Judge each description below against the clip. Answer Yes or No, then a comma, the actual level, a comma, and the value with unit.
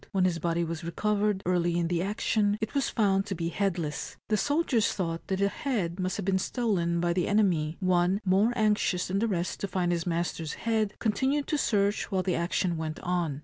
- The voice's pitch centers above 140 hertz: Yes, medium, 185 Hz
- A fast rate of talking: Yes, fast, 210 wpm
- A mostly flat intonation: No, average, 3.5 semitones